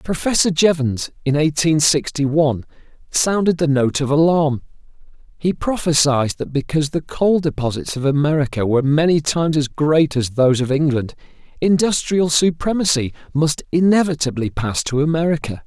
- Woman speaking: No, male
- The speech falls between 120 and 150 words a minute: Yes, average, 140 wpm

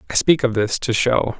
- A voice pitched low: Yes, low, 120 Hz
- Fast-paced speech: Yes, fast, 260 wpm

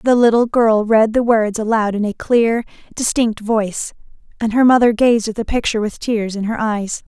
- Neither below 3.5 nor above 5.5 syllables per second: Yes, 5.0 syllables/s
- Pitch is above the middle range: Yes, high, 225 Hz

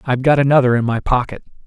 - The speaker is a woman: No, male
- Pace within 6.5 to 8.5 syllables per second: Yes, 7.6 syllables/s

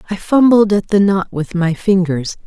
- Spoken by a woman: Yes, female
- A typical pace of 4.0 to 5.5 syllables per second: Yes, 4.6 syllables/s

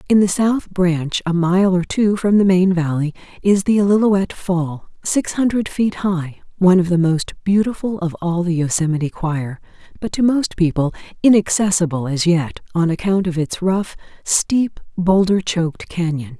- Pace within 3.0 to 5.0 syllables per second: Yes, 4.6 syllables/s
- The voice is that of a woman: Yes, female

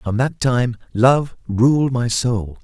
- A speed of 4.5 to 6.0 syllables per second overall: No, 3.0 syllables/s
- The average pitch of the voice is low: Yes, low, 120 Hz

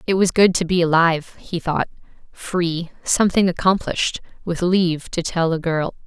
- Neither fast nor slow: Yes, average, 170 wpm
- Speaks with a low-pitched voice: No, medium, 175 Hz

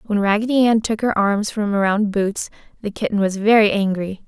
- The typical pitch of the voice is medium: No, high, 205 Hz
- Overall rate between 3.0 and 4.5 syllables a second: No, 5.2 syllables/s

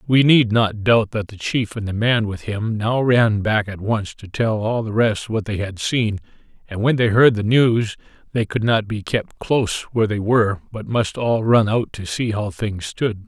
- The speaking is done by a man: Yes, male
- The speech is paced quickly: Yes, fast, 230 wpm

